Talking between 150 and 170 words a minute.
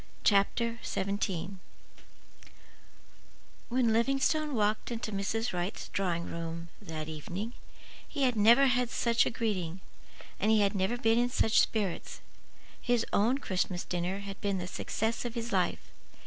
No: average, 140 wpm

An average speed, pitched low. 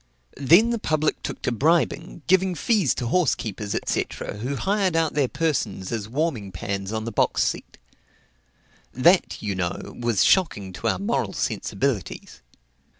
Yes: average, 150 wpm; low, 130 Hz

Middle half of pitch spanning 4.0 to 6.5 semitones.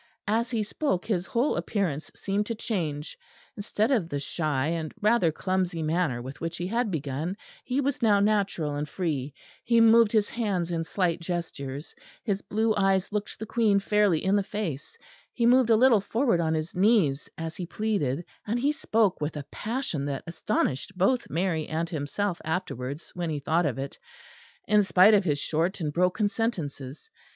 Yes: wide, 5.4 semitones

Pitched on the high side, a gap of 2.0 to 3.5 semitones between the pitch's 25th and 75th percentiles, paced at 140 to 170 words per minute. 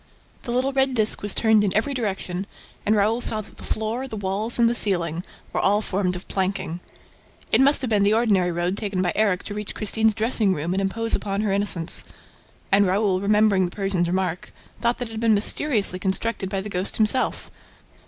No: high, 205 Hz; average, 2.8 semitones; fast, 205 wpm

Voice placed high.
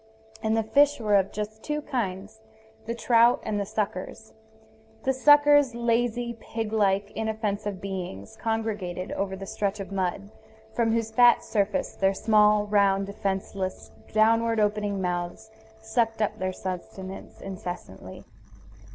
Yes: high, 210 Hz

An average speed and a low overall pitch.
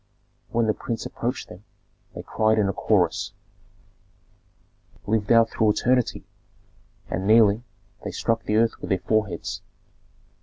No: slow, 130 wpm; low, 110 Hz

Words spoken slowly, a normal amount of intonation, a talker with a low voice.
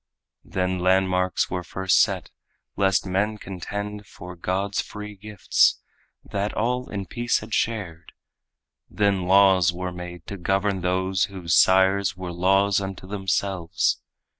No: slow, 130 wpm; narrow, 1.7 semitones; very low, 95 Hz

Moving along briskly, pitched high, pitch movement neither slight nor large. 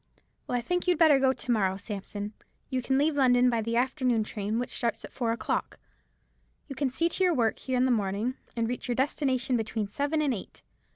Yes: fast, 220 wpm; high, 245 Hz; average, 3.3 semitones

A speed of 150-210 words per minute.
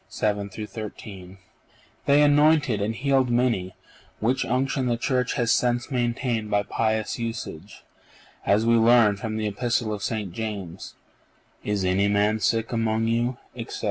No: average, 140 wpm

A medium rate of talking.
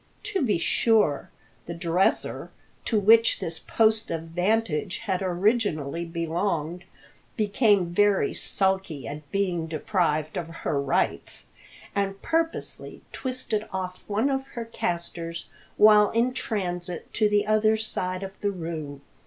No: slow, 130 wpm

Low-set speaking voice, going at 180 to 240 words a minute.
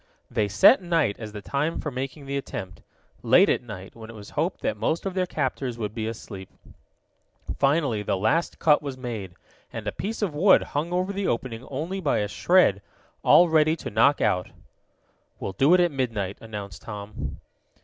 Yes: low, 130 Hz; average, 190 wpm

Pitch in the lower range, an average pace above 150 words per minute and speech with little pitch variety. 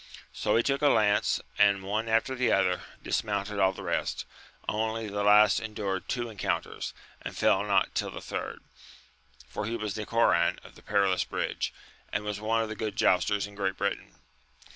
Yes: low, 105 Hz; average, 180 wpm; narrow, 1.9 semitones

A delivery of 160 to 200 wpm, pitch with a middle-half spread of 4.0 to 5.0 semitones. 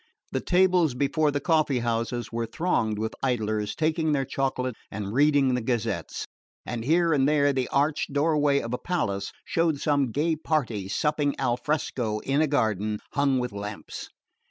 Yes: average, 165 wpm; average, 4.7 semitones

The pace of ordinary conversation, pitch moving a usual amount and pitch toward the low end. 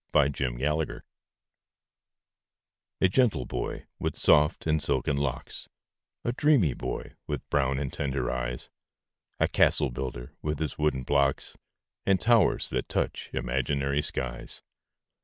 No: slow, 125 wpm; average, 3.0 semitones; very low, 70 Hz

